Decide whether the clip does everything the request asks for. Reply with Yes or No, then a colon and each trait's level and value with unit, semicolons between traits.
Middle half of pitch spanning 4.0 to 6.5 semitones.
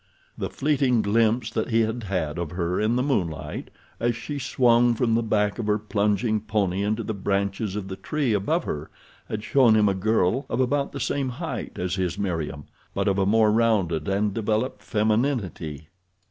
No: average, 3.3 semitones